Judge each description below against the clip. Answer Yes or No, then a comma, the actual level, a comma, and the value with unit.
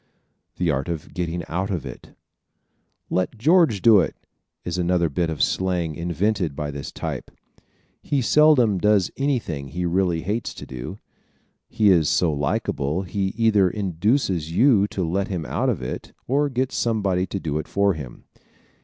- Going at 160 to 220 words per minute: Yes, average, 165 wpm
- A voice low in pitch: Yes, very low, 90 Hz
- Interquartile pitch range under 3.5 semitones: No, average, 4.5 semitones